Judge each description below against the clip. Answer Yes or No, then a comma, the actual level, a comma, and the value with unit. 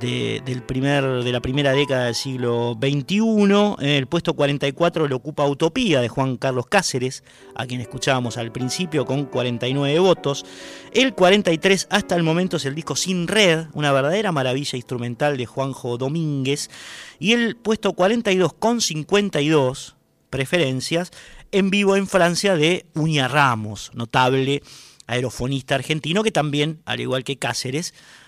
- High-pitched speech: No, medium, 140 Hz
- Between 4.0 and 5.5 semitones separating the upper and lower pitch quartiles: Yes, average, 5.1 semitones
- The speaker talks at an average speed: Yes, average, 145 wpm